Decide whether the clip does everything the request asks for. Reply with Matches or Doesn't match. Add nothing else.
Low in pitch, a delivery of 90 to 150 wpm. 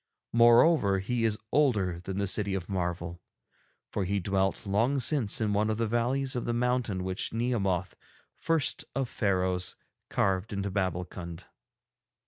Matches